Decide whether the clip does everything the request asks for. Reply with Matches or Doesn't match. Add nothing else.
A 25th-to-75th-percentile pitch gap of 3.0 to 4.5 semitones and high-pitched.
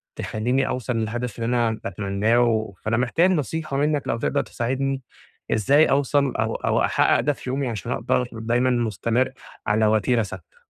Doesn't match